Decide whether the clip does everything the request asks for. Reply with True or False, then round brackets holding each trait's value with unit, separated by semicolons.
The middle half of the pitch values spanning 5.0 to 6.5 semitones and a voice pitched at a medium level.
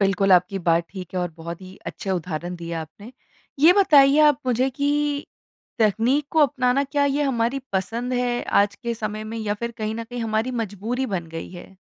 False (5.5 semitones; 225 Hz)